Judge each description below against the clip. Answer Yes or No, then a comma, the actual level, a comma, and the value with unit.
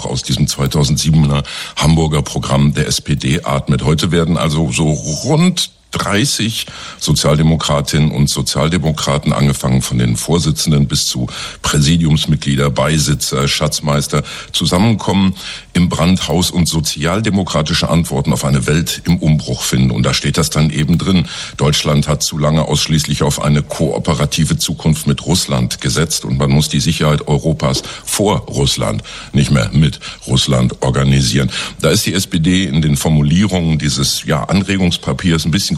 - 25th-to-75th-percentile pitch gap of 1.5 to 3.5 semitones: Yes, average, 2.9 semitones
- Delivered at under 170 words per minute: Yes, average, 140 wpm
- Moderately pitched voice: No, very low, 75 Hz